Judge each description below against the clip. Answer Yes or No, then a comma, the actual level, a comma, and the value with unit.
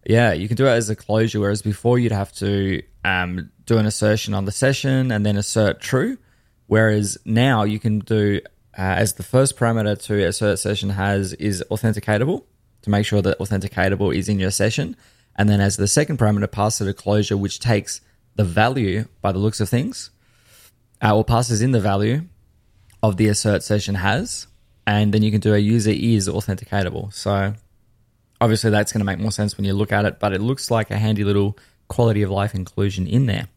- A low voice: Yes, low, 105 Hz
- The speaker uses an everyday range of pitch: No, narrow, 2.0 semitones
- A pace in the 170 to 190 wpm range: No, fast, 205 wpm